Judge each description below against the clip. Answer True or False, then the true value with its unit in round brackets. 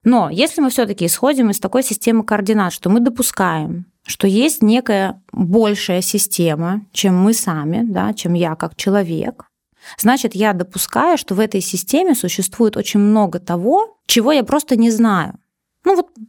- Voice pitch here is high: True (210 Hz)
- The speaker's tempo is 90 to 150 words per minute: False (160 wpm)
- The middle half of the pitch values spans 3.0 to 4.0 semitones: False (4.4 semitones)